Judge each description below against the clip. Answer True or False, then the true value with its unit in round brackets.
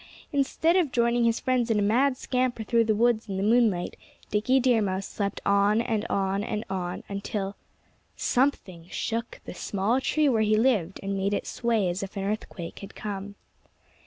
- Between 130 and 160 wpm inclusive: False (185 wpm)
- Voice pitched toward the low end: False (215 Hz)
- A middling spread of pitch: True (3.4 semitones)